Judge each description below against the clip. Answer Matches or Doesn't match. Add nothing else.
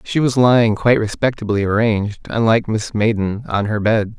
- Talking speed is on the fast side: Doesn't match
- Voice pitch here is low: Matches